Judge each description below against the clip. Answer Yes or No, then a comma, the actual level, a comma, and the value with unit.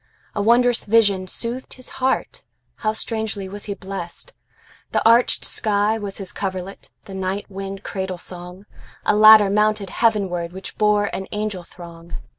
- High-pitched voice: Yes, high, 200 Hz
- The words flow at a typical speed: No, slow, 125 wpm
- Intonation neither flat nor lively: No, narrow, 2.3 semitones